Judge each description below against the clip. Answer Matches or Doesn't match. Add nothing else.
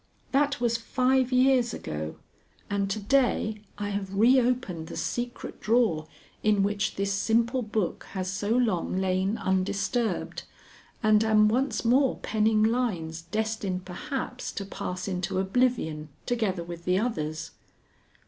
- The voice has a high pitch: Matches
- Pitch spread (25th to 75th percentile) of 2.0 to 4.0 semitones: Doesn't match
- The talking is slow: Matches